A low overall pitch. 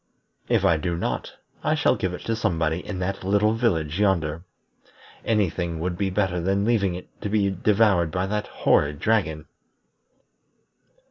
Yes: very low, 95 Hz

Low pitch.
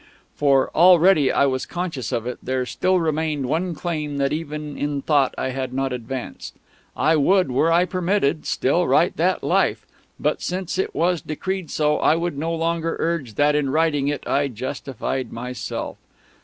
No: medium, 150 Hz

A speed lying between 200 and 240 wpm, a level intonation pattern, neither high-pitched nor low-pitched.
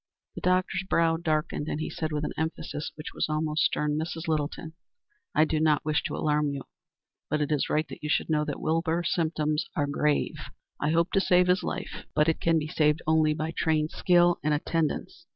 Yes: fast, 205 wpm; narrow, 1.5 semitones; medium, 155 Hz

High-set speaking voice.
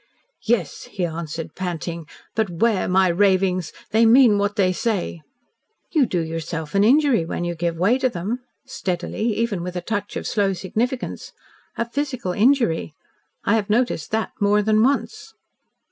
Yes: high, 200 Hz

